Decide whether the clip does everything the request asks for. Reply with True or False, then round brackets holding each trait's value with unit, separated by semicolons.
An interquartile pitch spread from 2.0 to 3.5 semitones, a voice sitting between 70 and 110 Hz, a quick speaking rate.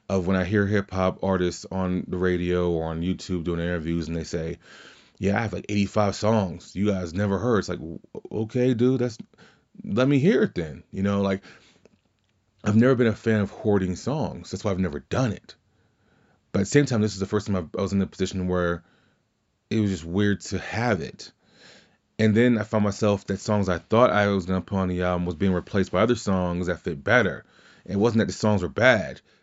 True (2.9 semitones; 100 Hz; 225 wpm)